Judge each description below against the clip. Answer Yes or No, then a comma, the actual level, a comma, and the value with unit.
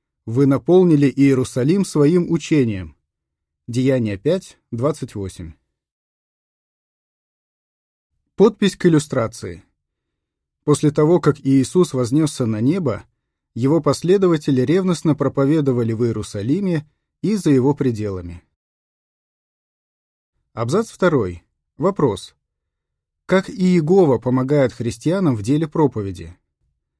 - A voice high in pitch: No, low, 135 Hz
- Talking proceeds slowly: Yes, slow, 85 wpm